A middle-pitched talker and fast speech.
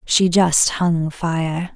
No: medium, 170 Hz; slow, 135 wpm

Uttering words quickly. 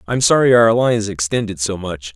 Yes: fast, 225 wpm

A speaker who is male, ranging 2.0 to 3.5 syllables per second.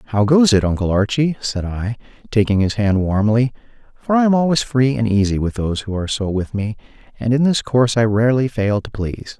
Yes: male; 2.1 syllables/s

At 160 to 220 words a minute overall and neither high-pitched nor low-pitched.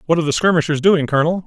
No: fast, 245 wpm; medium, 160 Hz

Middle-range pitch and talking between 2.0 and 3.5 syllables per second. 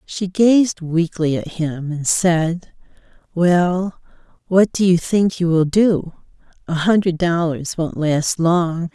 Yes: medium, 175 Hz; 3.3 syllables/s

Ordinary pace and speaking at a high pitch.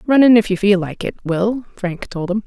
No: fast, 270 wpm; high, 205 Hz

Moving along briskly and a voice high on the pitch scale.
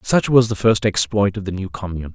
No: fast, 250 wpm; low, 100 Hz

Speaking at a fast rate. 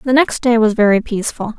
Yes: fast, 225 wpm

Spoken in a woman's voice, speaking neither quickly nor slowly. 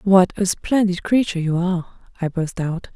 Yes: female; average, 185 wpm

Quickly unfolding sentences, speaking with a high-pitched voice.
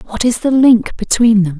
Yes: fast, 225 wpm; high, 225 Hz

